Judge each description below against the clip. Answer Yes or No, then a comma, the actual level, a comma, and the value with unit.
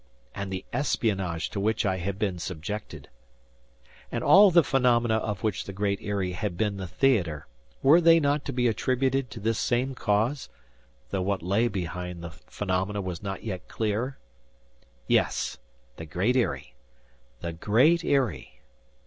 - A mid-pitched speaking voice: No, low, 105 Hz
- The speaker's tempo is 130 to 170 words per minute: Yes, average, 150 wpm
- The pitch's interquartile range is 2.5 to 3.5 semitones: No, average, 5.2 semitones